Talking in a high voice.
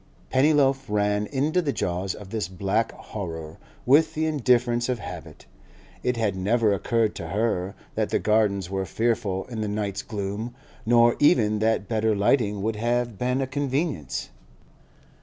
No: low, 110 Hz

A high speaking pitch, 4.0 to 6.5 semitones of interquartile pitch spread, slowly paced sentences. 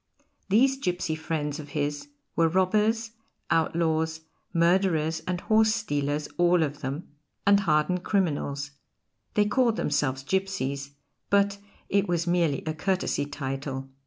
No: medium, 165 Hz; average, 4.9 semitones; slow, 125 wpm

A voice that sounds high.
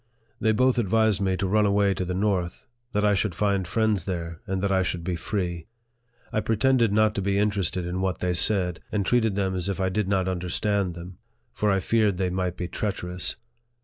No: very low, 95 Hz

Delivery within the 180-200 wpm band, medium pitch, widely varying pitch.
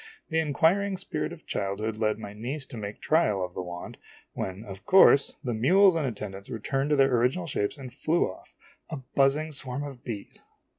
No: average, 190 wpm; low, 130 Hz; wide, 6.5 semitones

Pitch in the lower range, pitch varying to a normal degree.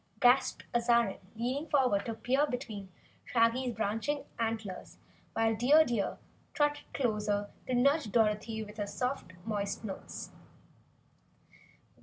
No: high, 230 Hz; average, 3.4 semitones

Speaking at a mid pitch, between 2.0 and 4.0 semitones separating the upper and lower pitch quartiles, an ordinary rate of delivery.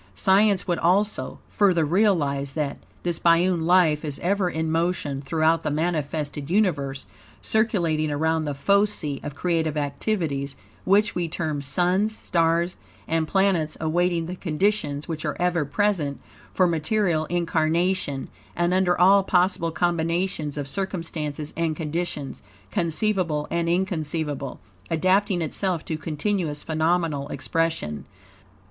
No: medium, 165 Hz; average, 3.2 semitones; slow, 125 wpm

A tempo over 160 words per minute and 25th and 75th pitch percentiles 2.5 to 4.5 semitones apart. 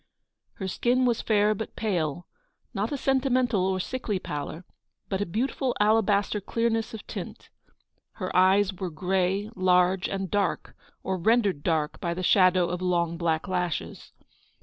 No: average, 155 wpm; average, 3.5 semitones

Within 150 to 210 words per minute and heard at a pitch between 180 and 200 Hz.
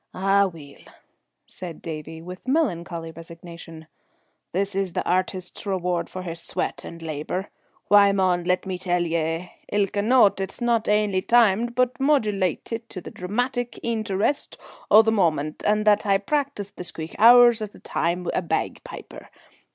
Yes: average, 160 wpm; high, 190 Hz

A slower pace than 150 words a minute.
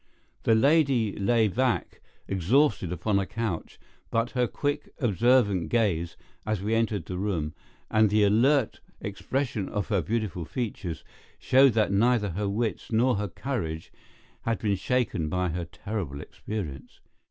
Yes: average, 140 wpm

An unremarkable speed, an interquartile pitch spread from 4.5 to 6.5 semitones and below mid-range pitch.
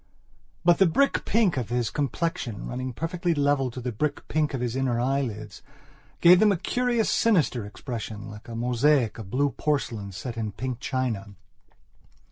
Yes: average, 160 wpm; average, 5.1 semitones; low, 130 Hz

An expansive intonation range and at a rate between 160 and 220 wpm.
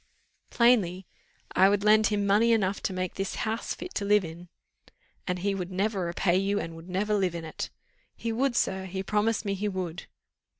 No: narrow, 2.5 semitones; average, 200 wpm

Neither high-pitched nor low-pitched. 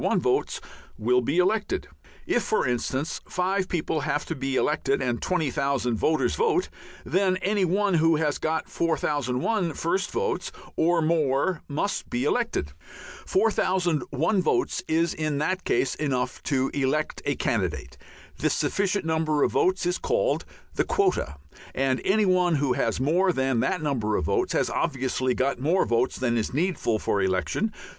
Yes: medium, 155 Hz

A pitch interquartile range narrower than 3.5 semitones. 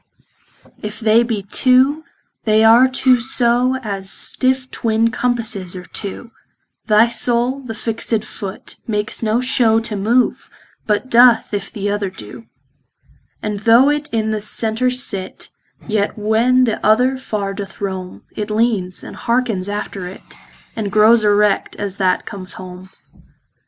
Yes: average, 3.1 semitones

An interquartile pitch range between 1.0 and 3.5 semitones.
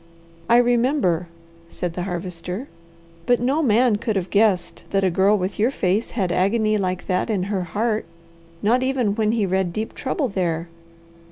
No: average, 4.3 semitones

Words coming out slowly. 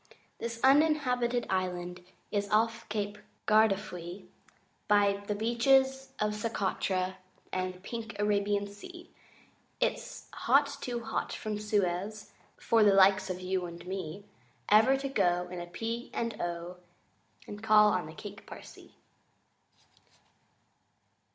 Yes: slow, 125 wpm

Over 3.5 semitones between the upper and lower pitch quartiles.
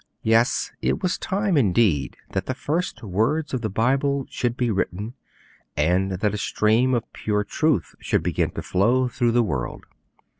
Yes: average, 4.7 semitones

